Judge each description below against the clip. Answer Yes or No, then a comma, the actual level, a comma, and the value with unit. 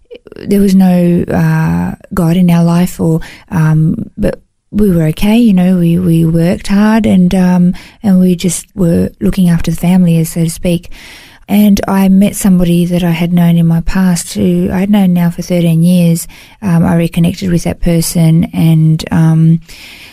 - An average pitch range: No, narrow, 2.2 semitones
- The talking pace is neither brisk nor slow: Yes, average, 180 wpm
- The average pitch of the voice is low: No, medium, 175 Hz